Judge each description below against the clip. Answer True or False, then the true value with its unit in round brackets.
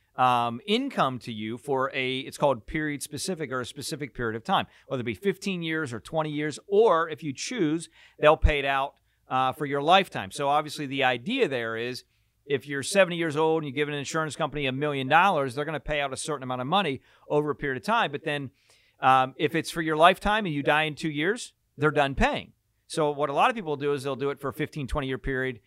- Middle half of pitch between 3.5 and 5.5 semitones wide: False (3.1 semitones)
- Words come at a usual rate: False (245 wpm)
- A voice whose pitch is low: False (145 Hz)